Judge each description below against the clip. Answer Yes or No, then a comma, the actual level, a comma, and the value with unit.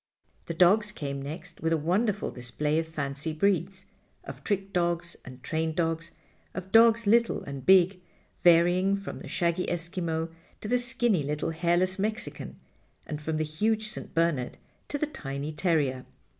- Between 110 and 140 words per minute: No, average, 155 wpm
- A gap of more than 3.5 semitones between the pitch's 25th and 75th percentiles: Yes, average, 4.0 semitones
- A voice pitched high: No, medium, 170 Hz